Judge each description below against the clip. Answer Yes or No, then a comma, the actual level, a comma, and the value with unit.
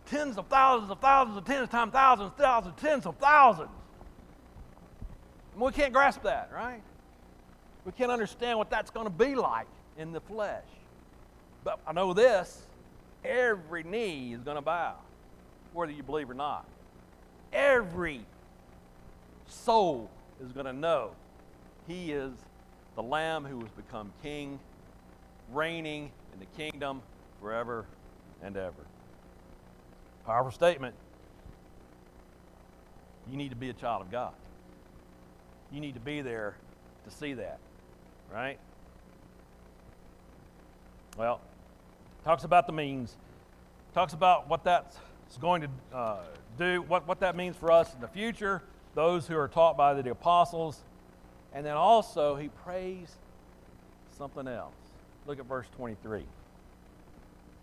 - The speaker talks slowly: Yes, slow, 130 wpm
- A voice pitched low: Yes, low, 115 Hz